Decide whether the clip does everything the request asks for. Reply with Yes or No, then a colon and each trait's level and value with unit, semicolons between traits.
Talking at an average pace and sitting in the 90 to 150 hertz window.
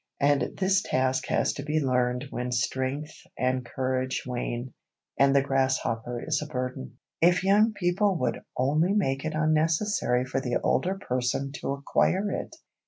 Yes: average, 155 wpm; low, 135 Hz